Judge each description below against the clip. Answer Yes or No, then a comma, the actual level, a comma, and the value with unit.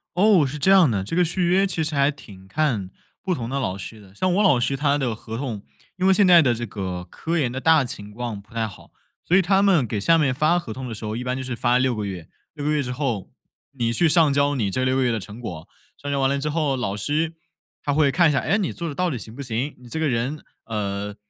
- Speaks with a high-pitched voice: No, low, 135 Hz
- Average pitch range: No, wide, 5.8 semitones